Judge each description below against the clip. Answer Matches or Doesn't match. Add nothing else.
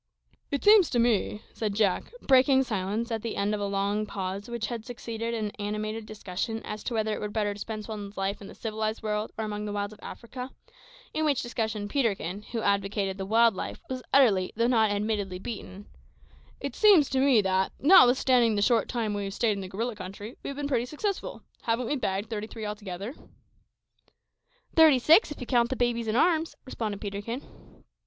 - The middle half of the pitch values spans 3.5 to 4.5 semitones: Doesn't match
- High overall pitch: Matches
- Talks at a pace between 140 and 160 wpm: Doesn't match